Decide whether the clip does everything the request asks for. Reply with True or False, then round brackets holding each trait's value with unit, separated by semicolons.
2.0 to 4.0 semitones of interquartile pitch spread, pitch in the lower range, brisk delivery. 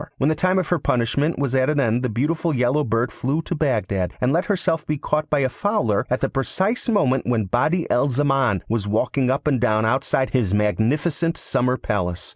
False (4.7 semitones; 130 Hz; 210 wpm)